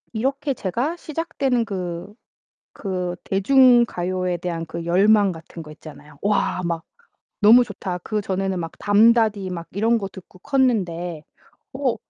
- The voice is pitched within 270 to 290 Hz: No, high, 195 Hz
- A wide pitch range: No, average, 4.9 semitones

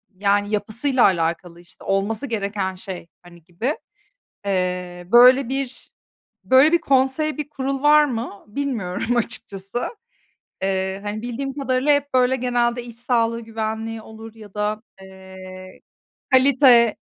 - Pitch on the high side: Yes, high, 225 Hz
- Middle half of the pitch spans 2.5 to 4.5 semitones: No, average, 5.1 semitones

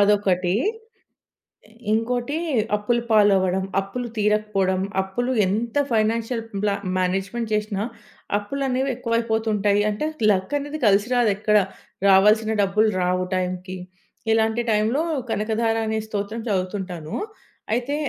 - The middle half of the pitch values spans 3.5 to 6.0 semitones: No, average, 2.8 semitones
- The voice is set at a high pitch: Yes, high, 210 Hz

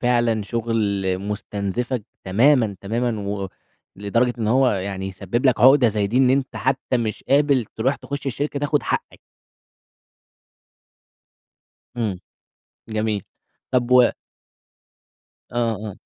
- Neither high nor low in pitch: No, low, 115 Hz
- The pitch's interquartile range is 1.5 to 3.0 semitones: No, average, 3.8 semitones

